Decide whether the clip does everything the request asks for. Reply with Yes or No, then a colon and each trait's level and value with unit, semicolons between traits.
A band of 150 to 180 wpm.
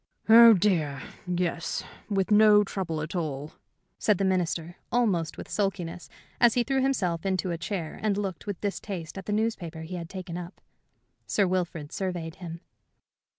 Yes: average, 160 wpm